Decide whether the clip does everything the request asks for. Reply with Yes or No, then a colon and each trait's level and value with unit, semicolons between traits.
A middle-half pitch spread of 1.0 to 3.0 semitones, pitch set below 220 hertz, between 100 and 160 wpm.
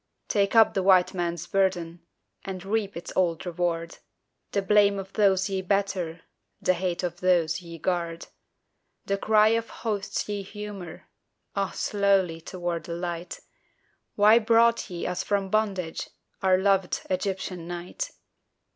Yes: narrow, 2.5 semitones; high, 190 Hz; average, 140 wpm